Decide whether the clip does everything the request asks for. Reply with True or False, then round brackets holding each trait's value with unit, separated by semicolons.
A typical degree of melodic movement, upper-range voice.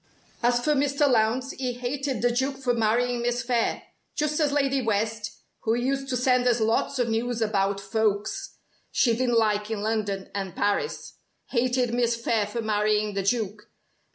True (3.1 semitones; 235 Hz)